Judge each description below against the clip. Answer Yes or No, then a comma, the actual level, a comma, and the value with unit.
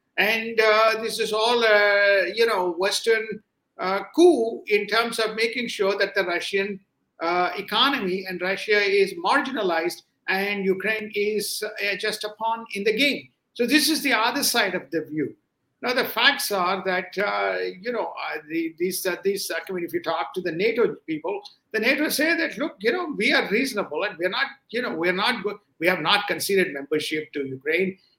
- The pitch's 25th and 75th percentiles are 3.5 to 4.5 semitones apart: Yes, average, 4.0 semitones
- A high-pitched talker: Yes, high, 205 Hz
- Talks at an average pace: Yes, average, 195 wpm